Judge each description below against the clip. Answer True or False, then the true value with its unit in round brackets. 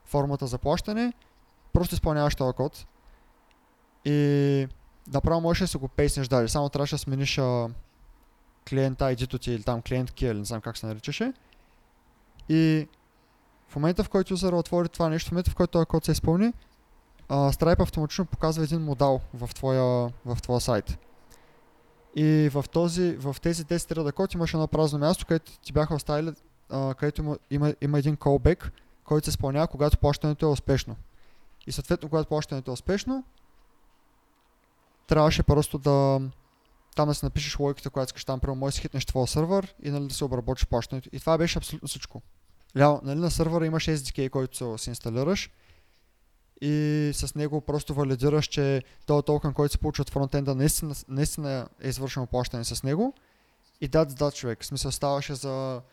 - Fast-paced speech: True (175 wpm)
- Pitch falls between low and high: True (145 Hz)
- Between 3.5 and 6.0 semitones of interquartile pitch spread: False (2.9 semitones)